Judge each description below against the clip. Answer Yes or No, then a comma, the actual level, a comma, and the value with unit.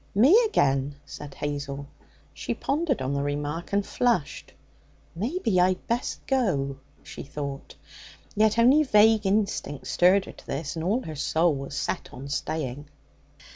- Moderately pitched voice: Yes, medium, 165 Hz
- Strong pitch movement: Yes, wide, 7.5 semitones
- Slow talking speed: No, average, 145 wpm